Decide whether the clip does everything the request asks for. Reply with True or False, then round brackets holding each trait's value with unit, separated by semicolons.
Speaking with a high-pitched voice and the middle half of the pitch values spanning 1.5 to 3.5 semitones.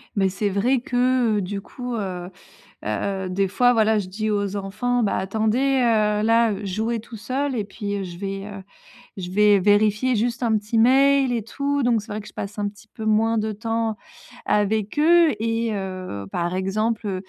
True (215 Hz; 2.8 semitones)